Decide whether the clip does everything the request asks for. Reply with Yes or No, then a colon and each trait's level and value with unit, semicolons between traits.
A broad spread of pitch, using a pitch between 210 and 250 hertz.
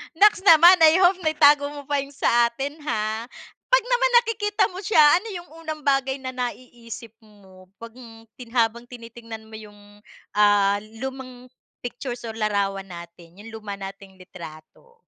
Yes: wide, 5.9 semitones; high, 245 Hz